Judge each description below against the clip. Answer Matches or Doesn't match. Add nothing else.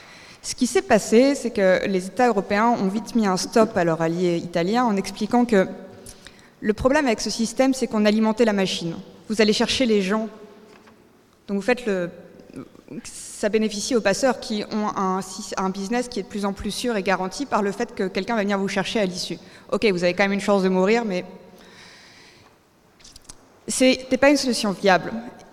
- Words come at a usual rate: Matches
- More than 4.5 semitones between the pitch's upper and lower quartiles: Doesn't match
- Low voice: Doesn't match